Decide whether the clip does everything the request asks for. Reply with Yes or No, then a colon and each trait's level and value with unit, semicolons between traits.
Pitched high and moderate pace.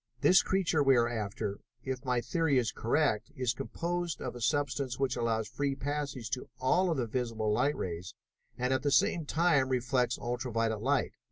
No: low, 130 Hz; average, 185 wpm